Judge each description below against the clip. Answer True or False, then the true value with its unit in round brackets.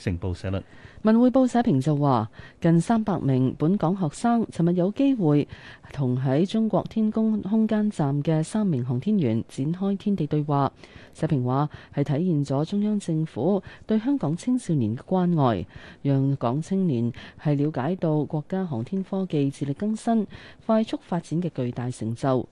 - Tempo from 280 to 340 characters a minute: False (245 characters per minute)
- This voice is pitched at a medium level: True (155 Hz)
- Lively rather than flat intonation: True (6.9 semitones)